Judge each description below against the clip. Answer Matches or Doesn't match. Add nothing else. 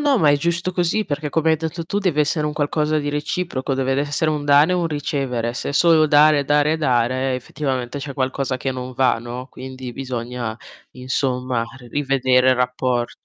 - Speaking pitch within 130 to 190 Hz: Matches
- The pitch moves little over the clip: Doesn't match